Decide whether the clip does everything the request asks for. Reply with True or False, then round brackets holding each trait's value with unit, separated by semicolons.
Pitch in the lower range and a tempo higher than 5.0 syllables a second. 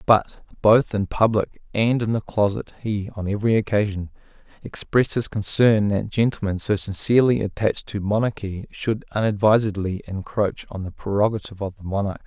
True (105 Hz; 5.3 syllables/s)